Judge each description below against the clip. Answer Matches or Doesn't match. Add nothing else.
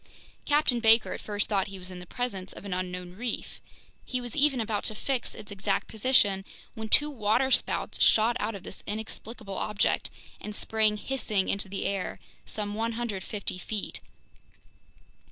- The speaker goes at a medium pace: Matches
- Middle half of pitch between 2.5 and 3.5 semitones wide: Matches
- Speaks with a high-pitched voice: Matches